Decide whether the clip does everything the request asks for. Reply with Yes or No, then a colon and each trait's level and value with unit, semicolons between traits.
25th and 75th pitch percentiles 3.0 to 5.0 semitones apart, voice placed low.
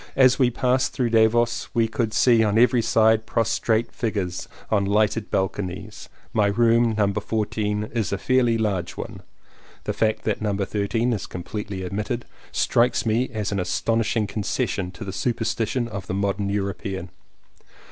No: narrow, 2.6 semitones; low, 110 Hz